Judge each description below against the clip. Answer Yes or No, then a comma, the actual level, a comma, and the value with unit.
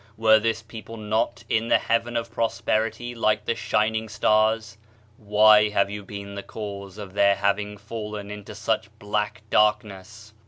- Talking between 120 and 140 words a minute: No, average, 160 wpm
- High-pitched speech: No, low, 105 Hz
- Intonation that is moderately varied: No, narrow, 1.4 semitones